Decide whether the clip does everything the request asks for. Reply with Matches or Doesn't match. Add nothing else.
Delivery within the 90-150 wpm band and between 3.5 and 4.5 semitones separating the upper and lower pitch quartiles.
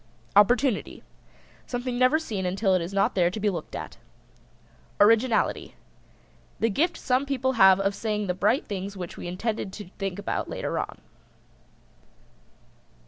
Matches